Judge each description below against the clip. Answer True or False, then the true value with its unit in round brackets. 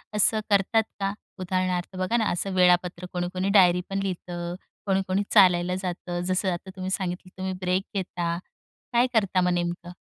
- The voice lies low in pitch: False (185 Hz)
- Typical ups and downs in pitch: False (1.5 semitones)